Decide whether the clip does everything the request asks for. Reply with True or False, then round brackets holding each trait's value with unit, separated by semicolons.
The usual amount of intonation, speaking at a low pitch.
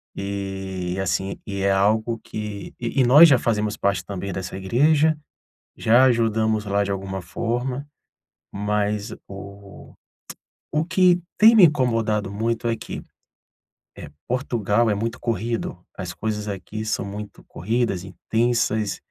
True (3.2 semitones; 105 Hz)